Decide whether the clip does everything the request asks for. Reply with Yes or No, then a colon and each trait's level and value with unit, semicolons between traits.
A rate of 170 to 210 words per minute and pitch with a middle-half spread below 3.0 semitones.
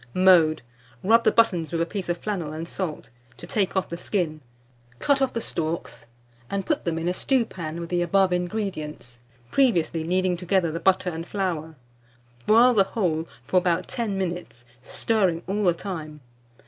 No: average, 175 wpm; average, 3.3 semitones